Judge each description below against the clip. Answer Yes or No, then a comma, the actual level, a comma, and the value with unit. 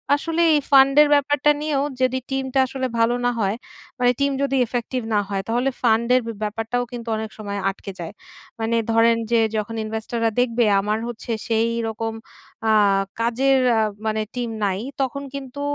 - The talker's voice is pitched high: Yes, high, 235 Hz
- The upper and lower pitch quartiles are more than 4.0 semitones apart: No, average, 3.2 semitones